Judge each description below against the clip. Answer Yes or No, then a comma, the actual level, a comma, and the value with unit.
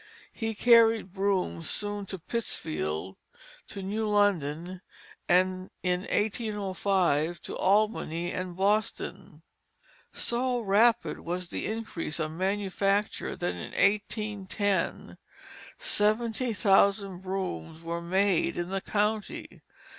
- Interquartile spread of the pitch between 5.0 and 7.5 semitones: No, average, 3.1 semitones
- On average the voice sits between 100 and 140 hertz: No, high, 195 Hz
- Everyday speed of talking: No, slow, 100 wpm